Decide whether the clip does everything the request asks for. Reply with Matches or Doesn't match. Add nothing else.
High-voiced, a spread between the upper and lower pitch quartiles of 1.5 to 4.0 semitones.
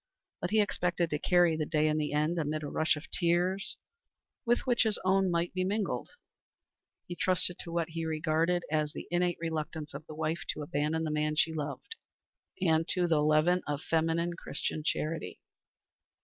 Doesn't match